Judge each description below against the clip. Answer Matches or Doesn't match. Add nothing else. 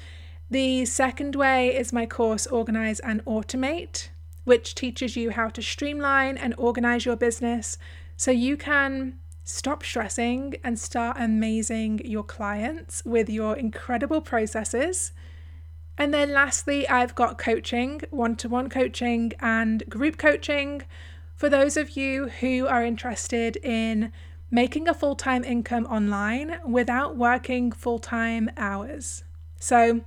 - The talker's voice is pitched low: Doesn't match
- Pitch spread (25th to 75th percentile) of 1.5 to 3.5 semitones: Matches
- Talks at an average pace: Doesn't match